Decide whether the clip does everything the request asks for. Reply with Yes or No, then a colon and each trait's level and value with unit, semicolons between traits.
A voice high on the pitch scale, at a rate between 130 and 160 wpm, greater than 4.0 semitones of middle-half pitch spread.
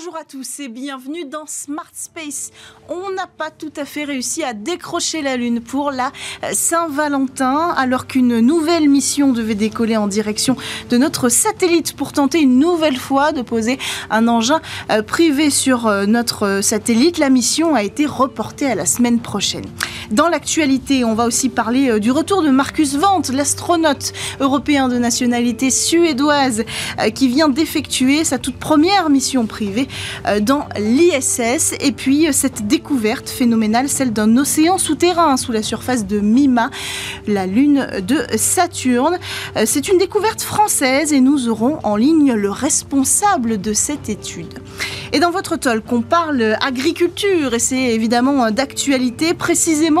Yes: very high, 275 Hz; average, 150 wpm; average, 4.6 semitones